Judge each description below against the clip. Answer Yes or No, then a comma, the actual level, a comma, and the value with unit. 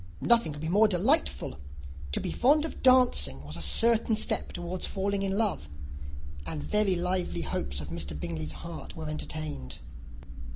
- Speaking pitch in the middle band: Yes, medium, 160 Hz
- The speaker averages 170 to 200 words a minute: No, average, 160 wpm